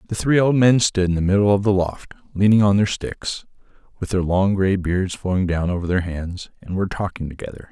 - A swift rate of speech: Yes, fast, 250 wpm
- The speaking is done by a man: Yes, male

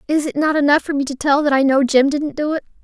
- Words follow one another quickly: Yes, fast, 315 wpm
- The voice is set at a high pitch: Yes, very high, 285 Hz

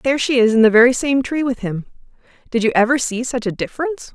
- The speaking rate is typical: No, fast, 245 wpm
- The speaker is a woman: Yes, female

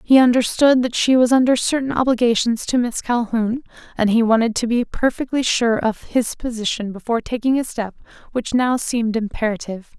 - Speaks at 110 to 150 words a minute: No, average, 175 wpm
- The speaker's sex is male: No, female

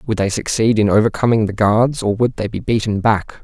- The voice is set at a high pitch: No, low, 110 Hz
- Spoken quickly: Yes, fast, 225 wpm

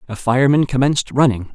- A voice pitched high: No, low, 130 Hz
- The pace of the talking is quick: No, average, 155 wpm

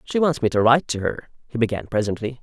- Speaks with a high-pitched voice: No, low, 120 Hz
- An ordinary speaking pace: No, fast, 250 wpm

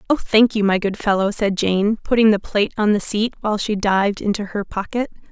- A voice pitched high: Yes, high, 210 Hz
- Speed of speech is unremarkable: No, fast, 225 wpm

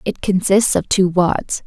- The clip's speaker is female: Yes, female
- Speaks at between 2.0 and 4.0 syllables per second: Yes, 3.8 syllables/s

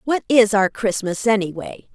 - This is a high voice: Yes, high, 210 Hz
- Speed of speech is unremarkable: Yes, average, 155 wpm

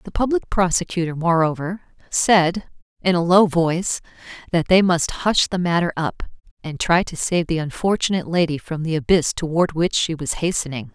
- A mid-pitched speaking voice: Yes, medium, 170 Hz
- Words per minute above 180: No, average, 170 wpm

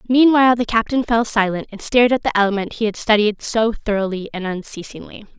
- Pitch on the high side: Yes, high, 215 Hz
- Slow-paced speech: No, average, 190 wpm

